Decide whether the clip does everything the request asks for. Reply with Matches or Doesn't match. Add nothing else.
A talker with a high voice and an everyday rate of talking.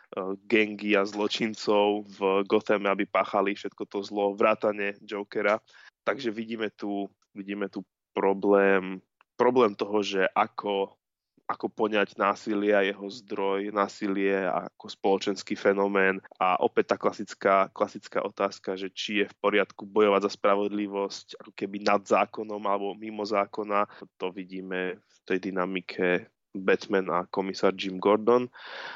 Doesn't match